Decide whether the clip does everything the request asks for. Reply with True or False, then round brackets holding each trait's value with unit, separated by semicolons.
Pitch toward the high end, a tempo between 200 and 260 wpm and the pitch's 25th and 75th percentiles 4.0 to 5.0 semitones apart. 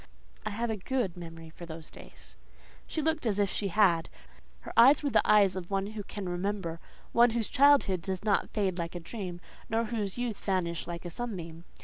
True (195 Hz; 205 wpm; 4.6 semitones)